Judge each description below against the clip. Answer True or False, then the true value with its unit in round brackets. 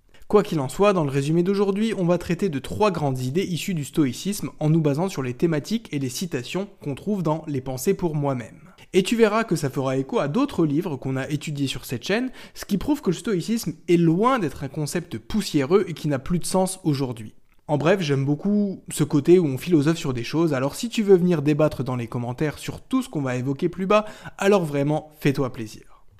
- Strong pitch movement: True (5.7 semitones)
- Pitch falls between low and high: True (160 Hz)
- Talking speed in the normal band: False (235 wpm)